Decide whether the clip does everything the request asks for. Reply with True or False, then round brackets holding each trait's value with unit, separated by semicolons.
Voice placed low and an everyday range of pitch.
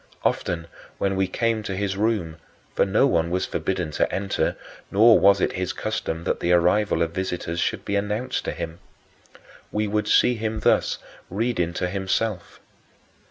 True (95 Hz; 3.4 semitones)